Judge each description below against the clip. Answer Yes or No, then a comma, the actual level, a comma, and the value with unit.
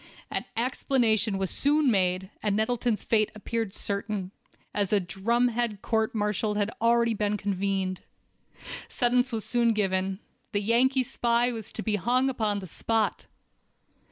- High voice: Yes, high, 220 Hz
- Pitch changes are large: No, average, 2.9 semitones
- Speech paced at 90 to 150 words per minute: Yes, slow, 135 wpm